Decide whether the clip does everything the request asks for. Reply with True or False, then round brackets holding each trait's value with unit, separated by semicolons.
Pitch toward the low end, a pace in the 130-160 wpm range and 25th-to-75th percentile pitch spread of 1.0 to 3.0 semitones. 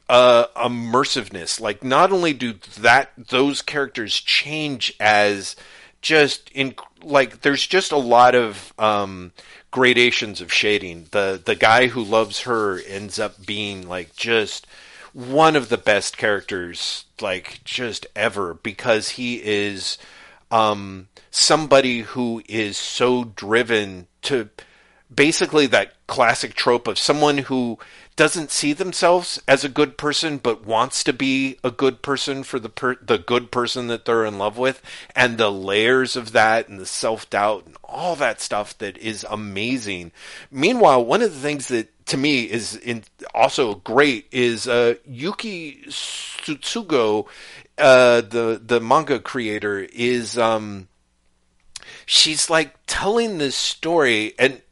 False (120 Hz; 140 wpm; 4.7 semitones)